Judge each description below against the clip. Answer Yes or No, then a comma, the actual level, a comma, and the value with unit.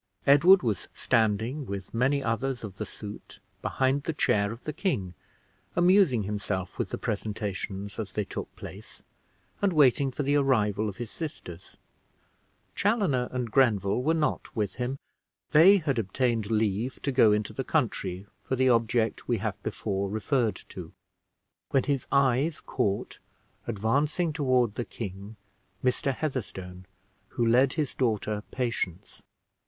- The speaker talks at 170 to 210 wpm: No, average, 145 wpm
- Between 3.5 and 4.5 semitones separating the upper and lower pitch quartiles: No, average, 4.9 semitones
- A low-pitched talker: Yes, low, 120 Hz